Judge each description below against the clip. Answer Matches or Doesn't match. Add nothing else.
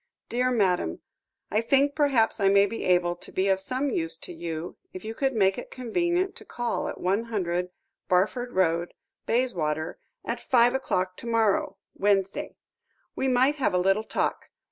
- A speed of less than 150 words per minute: Doesn't match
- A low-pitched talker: Doesn't match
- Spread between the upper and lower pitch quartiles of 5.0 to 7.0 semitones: Matches